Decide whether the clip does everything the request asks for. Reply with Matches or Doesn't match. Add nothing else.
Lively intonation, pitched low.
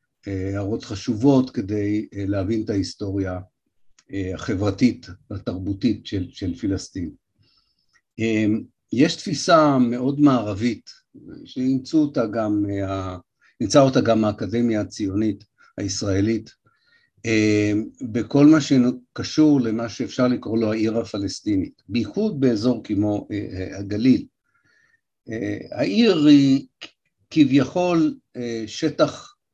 Matches